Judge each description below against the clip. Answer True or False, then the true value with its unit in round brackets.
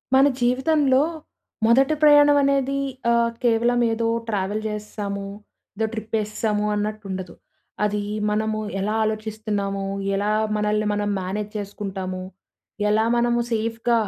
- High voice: True (215 Hz)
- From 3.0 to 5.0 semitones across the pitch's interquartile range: False (2.4 semitones)